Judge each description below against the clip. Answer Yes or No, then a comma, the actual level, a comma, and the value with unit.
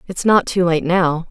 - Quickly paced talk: Yes, fast, 230 wpm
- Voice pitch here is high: No, medium, 175 Hz